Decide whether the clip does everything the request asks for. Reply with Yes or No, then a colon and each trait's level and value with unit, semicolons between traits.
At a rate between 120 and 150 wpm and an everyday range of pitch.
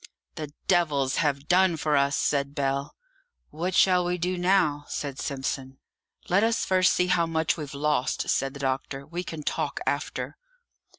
No: average, 165 wpm; average, 4.2 semitones